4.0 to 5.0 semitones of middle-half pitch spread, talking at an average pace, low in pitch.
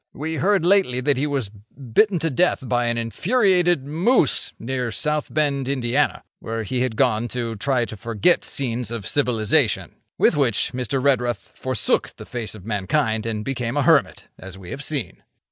Yes: average, 4.3 semitones; average, 175 wpm; low, 130 Hz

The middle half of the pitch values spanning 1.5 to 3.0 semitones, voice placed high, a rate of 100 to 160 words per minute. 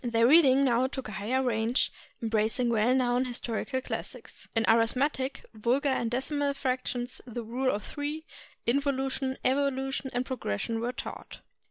Yes: narrow, 2.5 semitones; very high, 255 Hz; average, 155 wpm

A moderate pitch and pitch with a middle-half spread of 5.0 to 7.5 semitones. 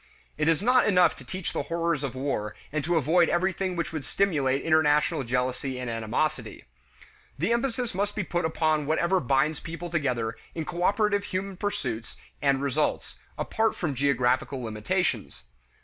Yes: medium, 155 Hz; average, 5.3 semitones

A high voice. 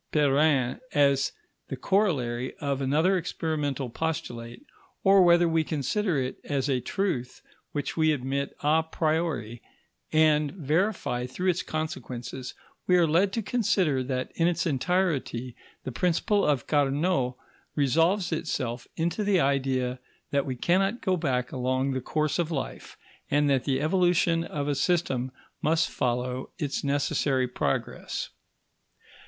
No: medium, 145 Hz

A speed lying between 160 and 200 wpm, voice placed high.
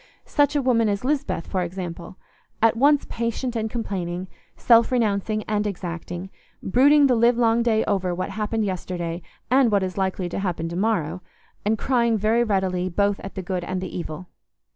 Yes: average, 170 wpm; high, 205 Hz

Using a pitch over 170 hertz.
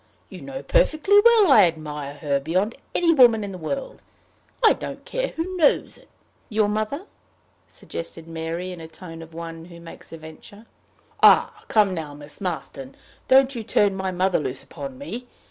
Yes: medium, 185 Hz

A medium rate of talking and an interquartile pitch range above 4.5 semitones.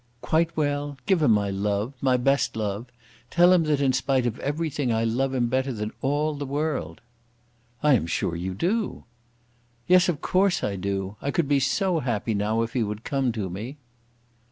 Yes: average, 190 wpm; wide, 5.6 semitones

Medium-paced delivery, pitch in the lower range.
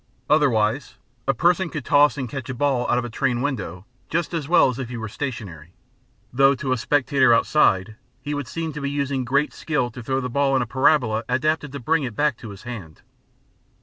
No: fast, 215 wpm; low, 130 Hz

